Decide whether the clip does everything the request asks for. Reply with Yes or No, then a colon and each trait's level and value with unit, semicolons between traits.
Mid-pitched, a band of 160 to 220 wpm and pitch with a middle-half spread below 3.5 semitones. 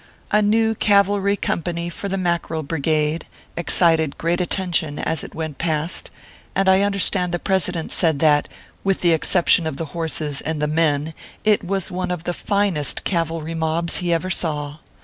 Yes: medium, 170 Hz; average, 170 wpm; average, 3.0 semitones